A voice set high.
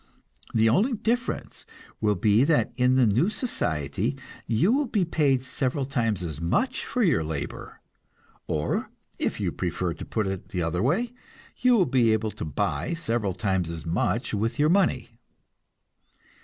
No: low, 115 Hz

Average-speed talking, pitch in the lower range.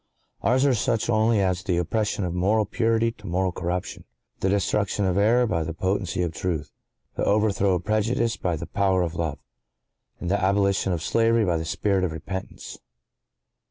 Yes: average, 165 wpm; very low, 95 Hz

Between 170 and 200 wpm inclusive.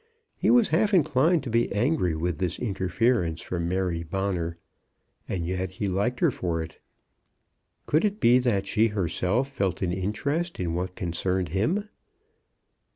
No: average, 155 wpm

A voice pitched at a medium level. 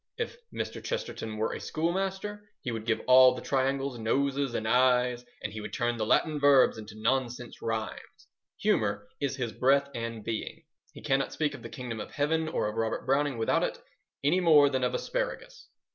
No: low, 130 Hz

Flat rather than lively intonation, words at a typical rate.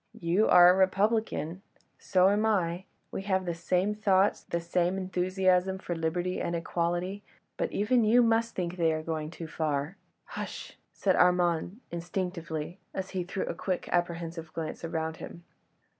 Yes: narrow, 2.3 semitones; average, 165 wpm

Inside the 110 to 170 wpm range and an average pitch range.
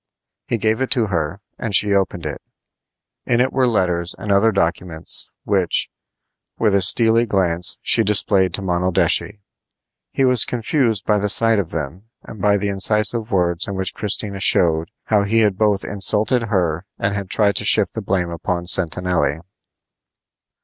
Yes: average, 165 wpm; average, 3.5 semitones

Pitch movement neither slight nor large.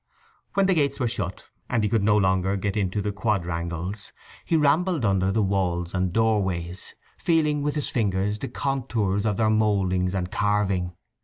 Yes: average, 3.5 semitones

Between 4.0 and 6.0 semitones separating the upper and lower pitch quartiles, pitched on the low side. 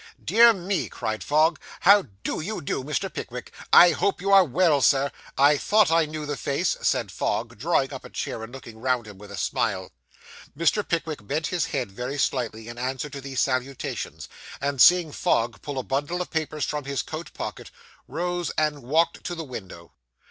No: average, 4.7 semitones; medium, 145 Hz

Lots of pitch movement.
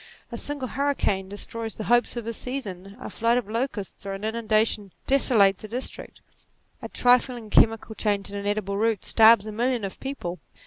No: average, 3.1 semitones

